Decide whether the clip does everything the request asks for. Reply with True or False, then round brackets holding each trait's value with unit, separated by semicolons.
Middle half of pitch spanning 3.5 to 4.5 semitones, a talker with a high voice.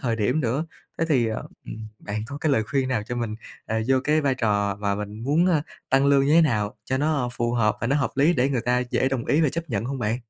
False (4.2 semitones; 125 Hz)